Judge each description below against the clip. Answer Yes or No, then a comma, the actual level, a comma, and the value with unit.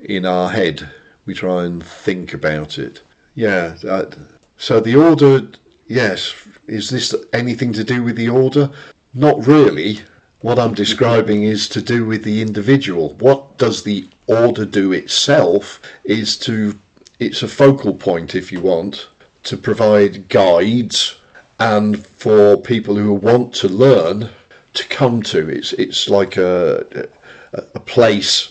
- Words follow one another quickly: No, average, 145 wpm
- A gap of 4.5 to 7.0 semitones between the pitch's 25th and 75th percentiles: No, average, 4.0 semitones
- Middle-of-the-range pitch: No, low, 110 Hz